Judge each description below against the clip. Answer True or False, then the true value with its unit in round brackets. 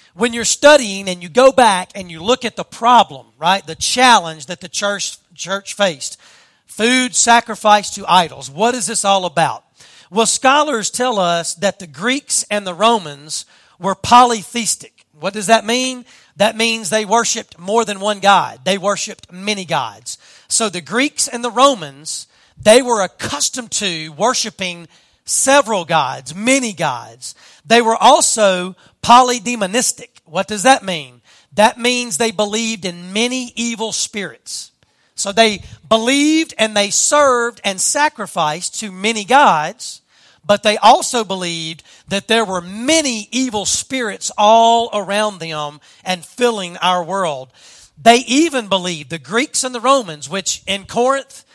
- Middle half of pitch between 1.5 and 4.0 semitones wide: False (4.8 semitones)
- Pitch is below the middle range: False (210 Hz)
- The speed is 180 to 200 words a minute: False (150 wpm)